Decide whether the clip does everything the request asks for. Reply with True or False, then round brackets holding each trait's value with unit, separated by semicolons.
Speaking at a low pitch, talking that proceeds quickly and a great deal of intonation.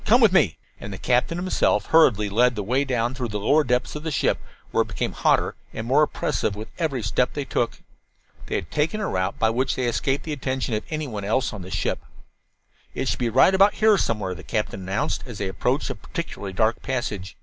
True (125 Hz; 225 wpm; 5.8 semitones)